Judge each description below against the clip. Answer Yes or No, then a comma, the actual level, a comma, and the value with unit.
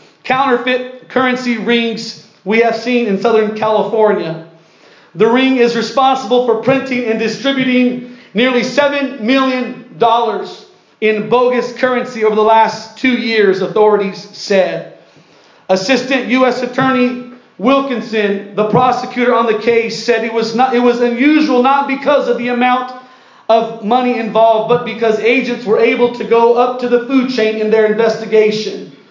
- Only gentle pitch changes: Yes, narrow, 2.3 semitones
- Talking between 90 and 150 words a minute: Yes, average, 145 wpm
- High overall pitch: Yes, high, 240 Hz